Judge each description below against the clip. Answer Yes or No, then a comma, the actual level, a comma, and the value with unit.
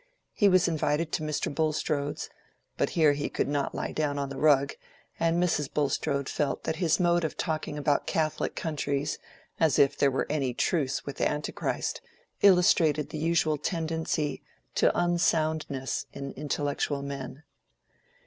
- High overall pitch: No, medium, 150 Hz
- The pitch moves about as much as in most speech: No, narrow, 2.3 semitones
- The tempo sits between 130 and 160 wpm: Yes, average, 150 wpm